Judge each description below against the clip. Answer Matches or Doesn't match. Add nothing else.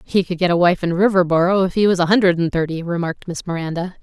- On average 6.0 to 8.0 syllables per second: Matches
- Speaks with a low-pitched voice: Doesn't match